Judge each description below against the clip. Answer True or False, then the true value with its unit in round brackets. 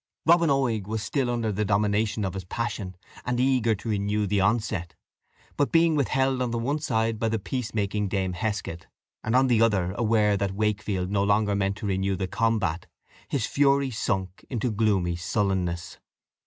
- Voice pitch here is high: False (105 Hz)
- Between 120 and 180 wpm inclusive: True (175 wpm)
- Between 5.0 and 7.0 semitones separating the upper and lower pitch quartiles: False (3.5 semitones)